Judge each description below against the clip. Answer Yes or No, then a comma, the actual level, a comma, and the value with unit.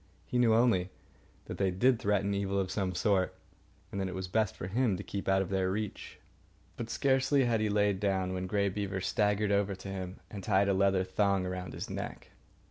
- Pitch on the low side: Yes, low, 100 Hz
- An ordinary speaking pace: No, fast, 210 wpm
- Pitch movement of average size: No, narrow, 1.9 semitones